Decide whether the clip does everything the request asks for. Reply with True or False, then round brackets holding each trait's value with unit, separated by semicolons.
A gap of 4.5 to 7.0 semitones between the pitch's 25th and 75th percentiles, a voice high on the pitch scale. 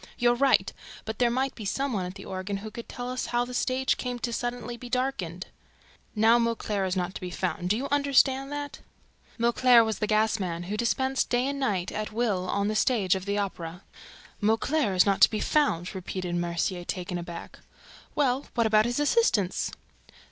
True (5.0 semitones; 220 Hz)